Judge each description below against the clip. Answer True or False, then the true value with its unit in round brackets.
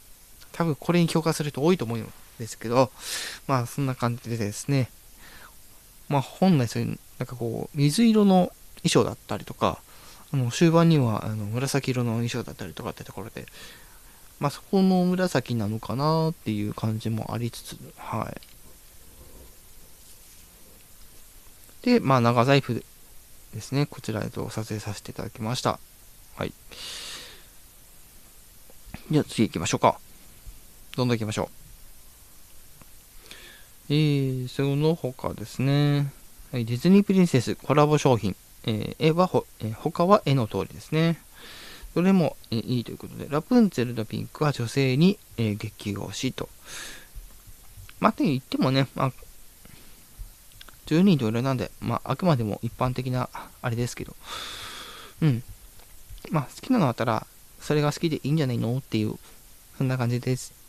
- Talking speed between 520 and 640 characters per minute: False (290 characters per minute)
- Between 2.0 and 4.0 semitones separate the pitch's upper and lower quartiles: False (5.1 semitones)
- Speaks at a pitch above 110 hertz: True (125 Hz)